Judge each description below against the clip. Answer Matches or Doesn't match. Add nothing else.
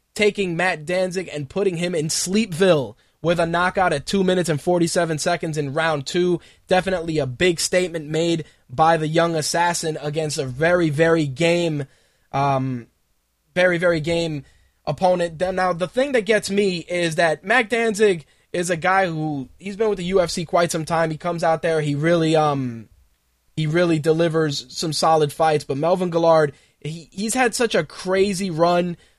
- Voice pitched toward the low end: Doesn't match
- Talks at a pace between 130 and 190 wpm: Matches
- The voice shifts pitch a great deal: Doesn't match